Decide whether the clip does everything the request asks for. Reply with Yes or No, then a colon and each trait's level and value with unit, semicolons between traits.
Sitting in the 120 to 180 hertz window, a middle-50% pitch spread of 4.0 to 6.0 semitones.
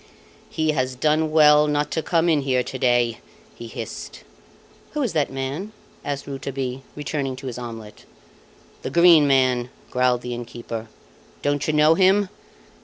No: medium, 140 Hz; average, 3.6 semitones